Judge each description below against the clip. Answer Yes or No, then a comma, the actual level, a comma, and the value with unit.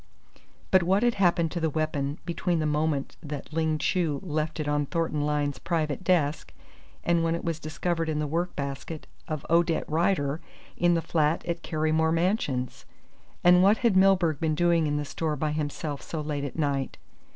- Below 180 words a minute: No, average, 185 wpm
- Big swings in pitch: No, narrow, 2.4 semitones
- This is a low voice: No, medium, 160 Hz